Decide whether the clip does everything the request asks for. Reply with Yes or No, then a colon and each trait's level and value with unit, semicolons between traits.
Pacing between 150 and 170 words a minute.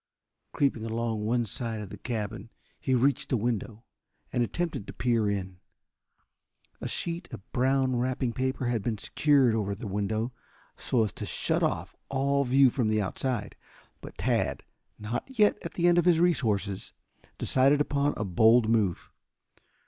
Yes: average, 160 wpm